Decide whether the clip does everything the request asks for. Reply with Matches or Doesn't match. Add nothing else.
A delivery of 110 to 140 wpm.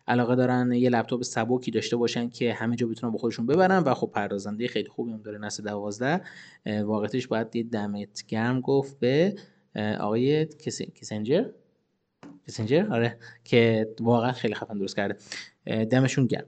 Doesn't match